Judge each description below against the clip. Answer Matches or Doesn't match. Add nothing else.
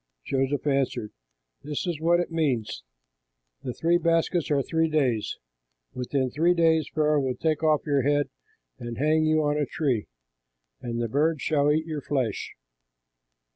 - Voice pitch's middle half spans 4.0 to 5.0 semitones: Doesn't match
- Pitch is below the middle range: Doesn't match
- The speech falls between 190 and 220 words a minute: Doesn't match